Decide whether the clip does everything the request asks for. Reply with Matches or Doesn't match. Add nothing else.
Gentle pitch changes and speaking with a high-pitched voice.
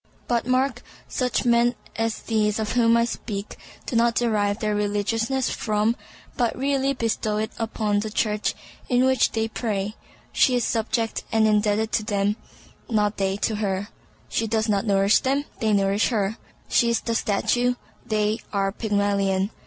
Matches